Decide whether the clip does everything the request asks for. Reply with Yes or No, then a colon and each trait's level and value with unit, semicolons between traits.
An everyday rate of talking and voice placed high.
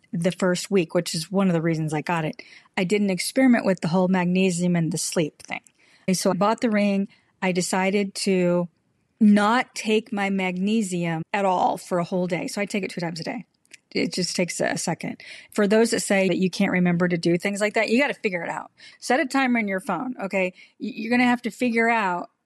No: fast, 230 wpm; high, 195 Hz